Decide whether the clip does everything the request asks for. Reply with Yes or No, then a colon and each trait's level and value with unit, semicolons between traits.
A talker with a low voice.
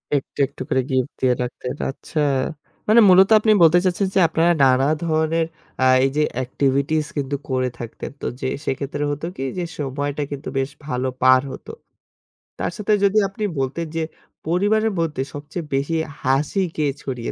No: medium, 145 Hz